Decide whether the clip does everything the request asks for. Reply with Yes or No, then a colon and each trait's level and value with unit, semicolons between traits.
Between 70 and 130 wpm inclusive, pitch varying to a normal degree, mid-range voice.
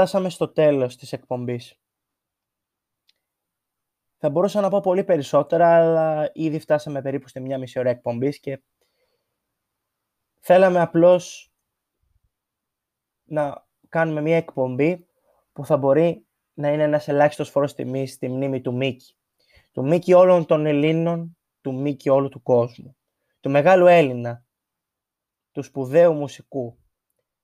Yes: average, 120 wpm; average, 3.8 semitones; medium, 150 Hz